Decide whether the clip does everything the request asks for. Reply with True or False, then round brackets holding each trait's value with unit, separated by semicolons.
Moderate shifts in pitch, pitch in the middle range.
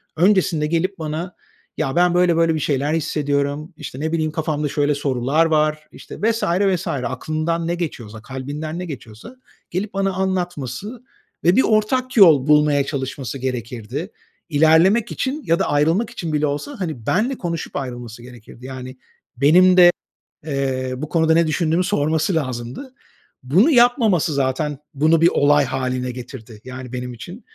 True (4.9 semitones; 155 Hz)